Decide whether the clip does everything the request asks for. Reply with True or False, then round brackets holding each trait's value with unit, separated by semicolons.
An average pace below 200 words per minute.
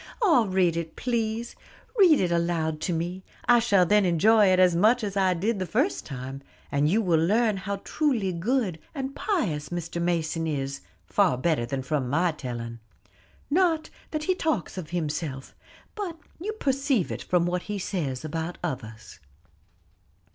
True (165 wpm)